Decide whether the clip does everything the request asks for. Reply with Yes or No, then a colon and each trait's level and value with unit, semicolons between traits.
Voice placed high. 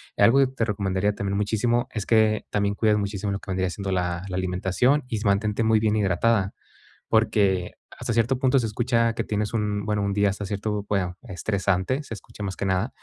No: low, 105 Hz